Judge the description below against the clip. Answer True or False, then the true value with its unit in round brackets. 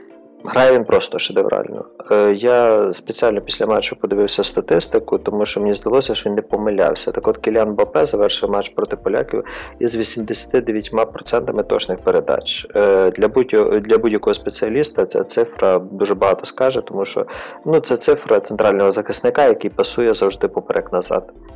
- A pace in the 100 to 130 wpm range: False (140 wpm)